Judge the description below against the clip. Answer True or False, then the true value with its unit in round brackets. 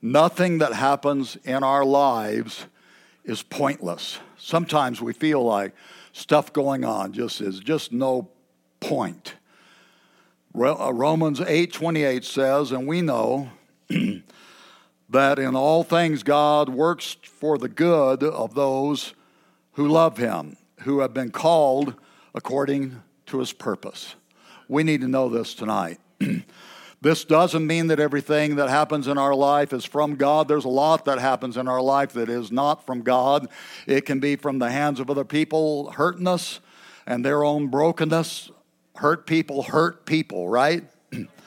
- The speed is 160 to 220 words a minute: False (145 wpm)